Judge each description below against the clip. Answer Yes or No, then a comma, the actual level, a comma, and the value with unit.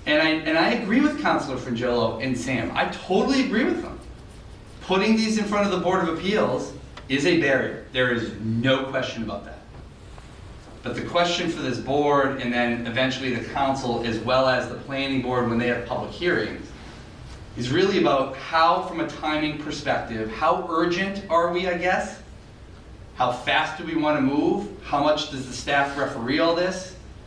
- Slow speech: No, average, 185 wpm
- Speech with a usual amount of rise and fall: No, wide, 7.0 semitones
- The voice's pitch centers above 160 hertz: No, medium, 140 Hz